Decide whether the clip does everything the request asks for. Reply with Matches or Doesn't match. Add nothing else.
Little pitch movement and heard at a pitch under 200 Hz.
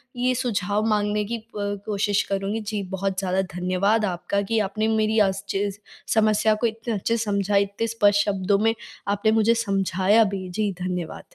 Doesn't match